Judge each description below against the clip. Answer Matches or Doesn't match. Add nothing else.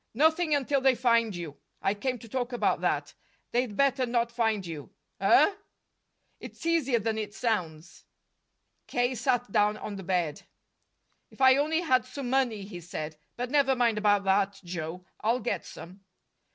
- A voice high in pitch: Matches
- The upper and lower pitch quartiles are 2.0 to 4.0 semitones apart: Doesn't match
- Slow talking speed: Doesn't match